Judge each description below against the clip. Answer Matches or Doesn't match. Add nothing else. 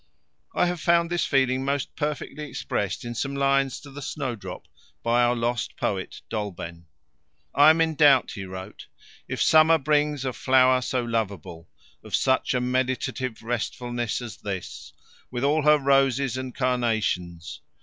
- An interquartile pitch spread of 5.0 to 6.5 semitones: Doesn't match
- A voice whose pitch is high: Doesn't match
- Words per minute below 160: Matches